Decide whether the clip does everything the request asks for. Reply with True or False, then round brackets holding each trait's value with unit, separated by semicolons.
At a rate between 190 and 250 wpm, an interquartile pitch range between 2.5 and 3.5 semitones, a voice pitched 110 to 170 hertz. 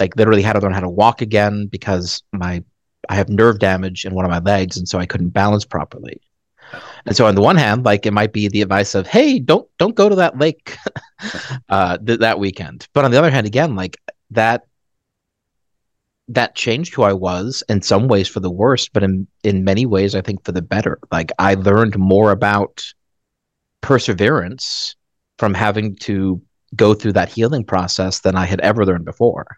False (200 wpm; 2.8 semitones; 100 Hz)